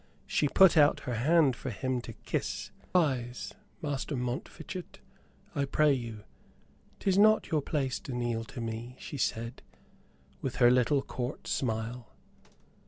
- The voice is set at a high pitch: No, low, 130 Hz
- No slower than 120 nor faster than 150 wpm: Yes, average, 140 wpm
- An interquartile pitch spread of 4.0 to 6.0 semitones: No, average, 3.6 semitones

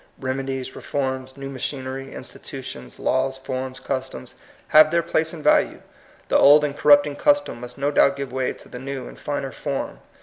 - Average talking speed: Yes, average, 175 wpm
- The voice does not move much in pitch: Yes, narrow, 1.6 semitones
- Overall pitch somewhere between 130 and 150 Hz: Yes, low, 135 Hz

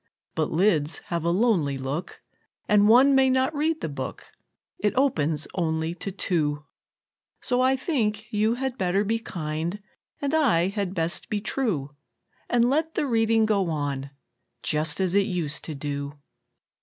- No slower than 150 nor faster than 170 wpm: Yes, average, 155 wpm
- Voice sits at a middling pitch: No, high, 195 Hz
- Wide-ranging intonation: Yes, wide, 7.2 semitones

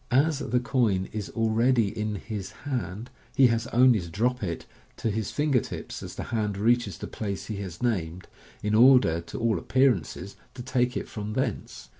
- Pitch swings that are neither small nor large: Yes, average, 3.7 semitones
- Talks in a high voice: No, low, 110 Hz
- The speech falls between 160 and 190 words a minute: Yes, average, 185 wpm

